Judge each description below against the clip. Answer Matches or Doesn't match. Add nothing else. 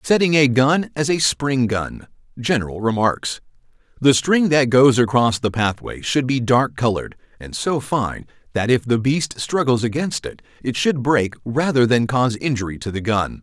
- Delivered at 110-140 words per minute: Doesn't match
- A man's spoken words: Matches